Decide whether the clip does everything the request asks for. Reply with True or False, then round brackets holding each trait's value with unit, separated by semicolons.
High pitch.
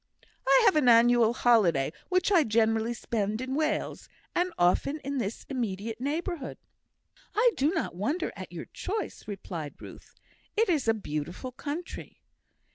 True (245 Hz)